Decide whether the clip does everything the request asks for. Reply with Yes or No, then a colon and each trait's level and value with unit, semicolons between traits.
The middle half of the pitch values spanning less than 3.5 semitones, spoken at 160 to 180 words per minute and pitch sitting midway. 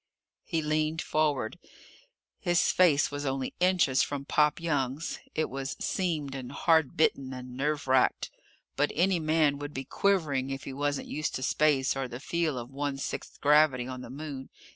Yes: average, 2.7 semitones; average, 170 wpm; medium, 145 Hz